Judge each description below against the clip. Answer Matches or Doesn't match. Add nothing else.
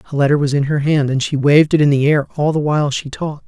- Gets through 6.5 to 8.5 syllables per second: Matches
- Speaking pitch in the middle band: Matches